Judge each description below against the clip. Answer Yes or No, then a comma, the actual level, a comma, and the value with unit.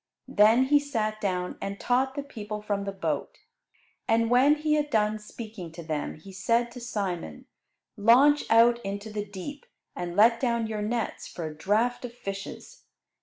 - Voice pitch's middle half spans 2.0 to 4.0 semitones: Yes, average, 3.6 semitones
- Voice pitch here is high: Yes, high, 220 Hz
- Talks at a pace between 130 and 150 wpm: No, average, 170 wpm